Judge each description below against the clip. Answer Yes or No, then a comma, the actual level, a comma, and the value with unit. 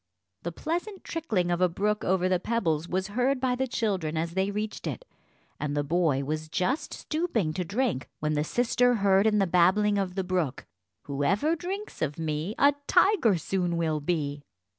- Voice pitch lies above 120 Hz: Yes, high, 190 Hz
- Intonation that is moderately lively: No, wide, 6.5 semitones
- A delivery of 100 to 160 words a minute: No, average, 185 wpm